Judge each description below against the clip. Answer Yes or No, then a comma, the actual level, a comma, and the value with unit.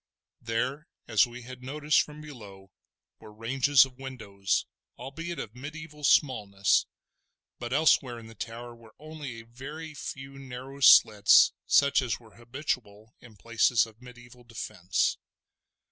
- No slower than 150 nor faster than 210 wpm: No, slow, 135 wpm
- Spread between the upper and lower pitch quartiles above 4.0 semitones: No, average, 3.4 semitones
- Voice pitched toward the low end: Yes, low, 125 Hz